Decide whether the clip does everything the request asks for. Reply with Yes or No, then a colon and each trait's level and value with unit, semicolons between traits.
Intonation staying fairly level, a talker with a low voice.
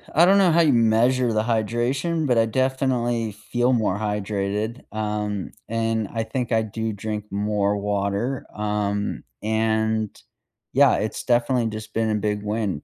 Yes: narrow, 2.3 semitones; low, 110 Hz